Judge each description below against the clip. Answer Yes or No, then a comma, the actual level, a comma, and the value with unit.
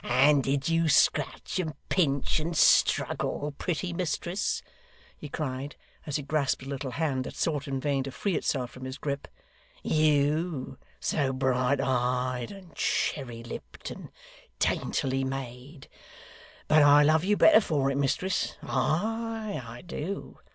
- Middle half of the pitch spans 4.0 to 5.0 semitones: No, average, 3.4 semitones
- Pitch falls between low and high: Yes, medium, 145 Hz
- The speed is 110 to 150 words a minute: Yes, average, 145 wpm